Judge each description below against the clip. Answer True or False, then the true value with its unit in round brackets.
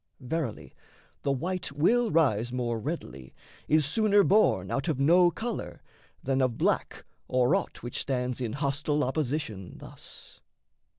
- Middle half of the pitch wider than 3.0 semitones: True (5.1 semitones)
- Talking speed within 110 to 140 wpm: True (135 wpm)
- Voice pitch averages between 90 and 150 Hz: True (140 Hz)